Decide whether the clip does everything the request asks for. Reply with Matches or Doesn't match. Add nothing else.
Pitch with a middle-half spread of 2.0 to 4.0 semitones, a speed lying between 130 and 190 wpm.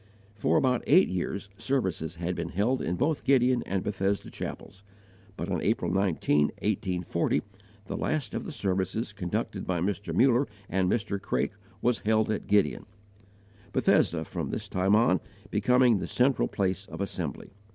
Doesn't match